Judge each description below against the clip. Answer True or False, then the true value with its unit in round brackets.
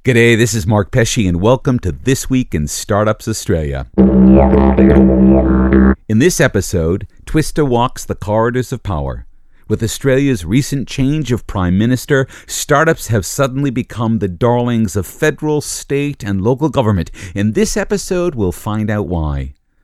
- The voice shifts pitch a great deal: True (6.8 semitones)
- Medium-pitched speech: False (110 Hz)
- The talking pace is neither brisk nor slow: True (145 wpm)